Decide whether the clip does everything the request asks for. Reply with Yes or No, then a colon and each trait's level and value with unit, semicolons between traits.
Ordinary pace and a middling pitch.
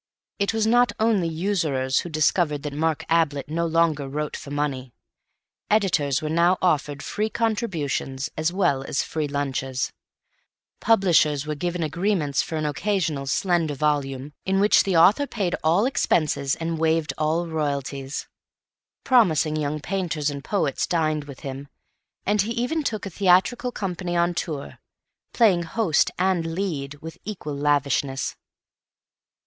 Yes: average, 145 wpm; medium, 160 Hz